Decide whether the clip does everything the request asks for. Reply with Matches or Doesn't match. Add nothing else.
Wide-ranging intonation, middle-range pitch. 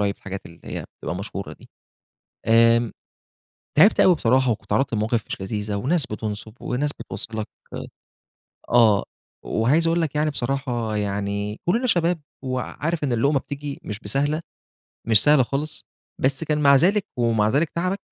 Doesn't match